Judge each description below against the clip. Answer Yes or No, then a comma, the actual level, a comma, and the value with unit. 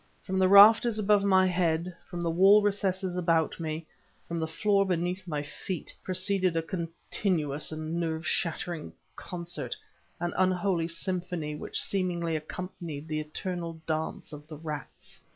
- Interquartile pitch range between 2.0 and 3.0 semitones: Yes, average, 2.7 semitones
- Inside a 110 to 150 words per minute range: Yes, average, 145 wpm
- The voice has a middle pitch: Yes, medium, 175 Hz